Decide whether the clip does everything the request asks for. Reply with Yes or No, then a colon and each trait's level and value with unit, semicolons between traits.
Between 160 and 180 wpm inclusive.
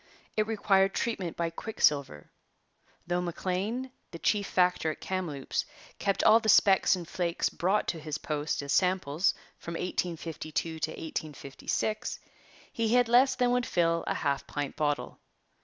No: average, 145 wpm